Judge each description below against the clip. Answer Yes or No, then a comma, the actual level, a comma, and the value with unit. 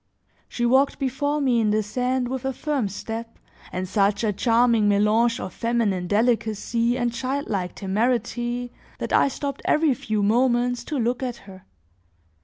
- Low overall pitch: No, high, 235 Hz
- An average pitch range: Yes, average, 3.2 semitones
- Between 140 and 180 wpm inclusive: Yes, average, 155 wpm